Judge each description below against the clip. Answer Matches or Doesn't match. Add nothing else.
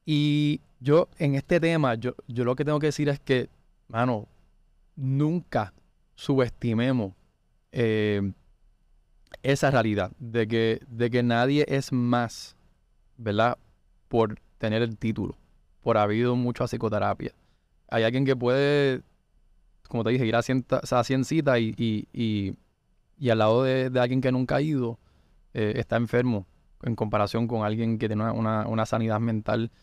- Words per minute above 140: Matches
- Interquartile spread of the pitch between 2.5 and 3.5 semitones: Matches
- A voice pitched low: Matches